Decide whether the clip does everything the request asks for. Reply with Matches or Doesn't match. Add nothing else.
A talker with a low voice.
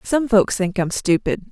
Doesn't match